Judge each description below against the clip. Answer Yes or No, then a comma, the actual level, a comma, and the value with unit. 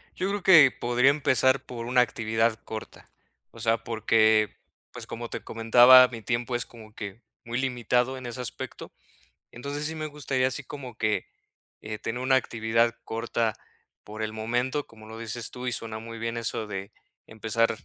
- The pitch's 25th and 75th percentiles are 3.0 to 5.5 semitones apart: No, narrow, 2.5 semitones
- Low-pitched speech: Yes, low, 115 Hz